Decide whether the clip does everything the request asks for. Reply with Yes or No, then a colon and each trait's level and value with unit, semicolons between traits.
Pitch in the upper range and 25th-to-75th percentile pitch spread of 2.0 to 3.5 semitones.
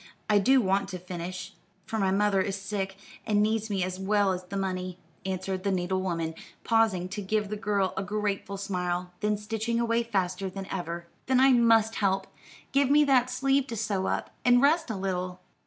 Yes: high, 200 Hz; average, 3.1 semitones